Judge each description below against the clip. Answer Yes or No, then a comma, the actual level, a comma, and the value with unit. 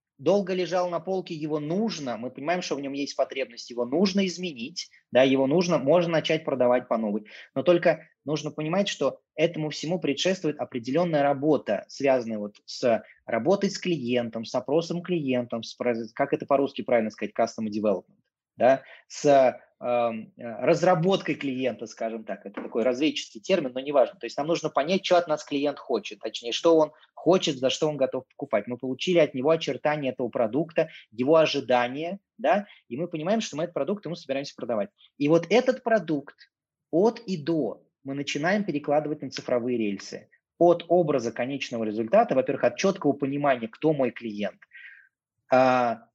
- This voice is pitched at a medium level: Yes, medium, 150 Hz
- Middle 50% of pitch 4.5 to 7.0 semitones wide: Yes, wide, 5.4 semitones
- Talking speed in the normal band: No, fast, 165 wpm